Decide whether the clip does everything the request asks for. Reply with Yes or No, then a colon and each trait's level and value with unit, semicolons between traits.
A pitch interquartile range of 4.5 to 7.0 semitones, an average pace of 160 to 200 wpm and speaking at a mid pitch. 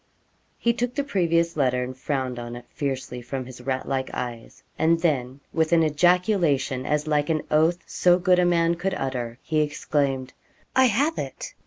Yes: average, 5.1 semitones; average, 180 wpm; medium, 150 Hz